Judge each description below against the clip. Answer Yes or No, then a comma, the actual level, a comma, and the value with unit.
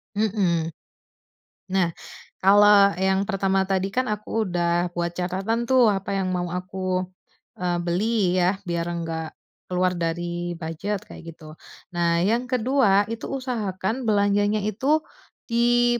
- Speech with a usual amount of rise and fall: Yes, average, 3.6 semitones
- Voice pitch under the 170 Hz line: No, high, 190 Hz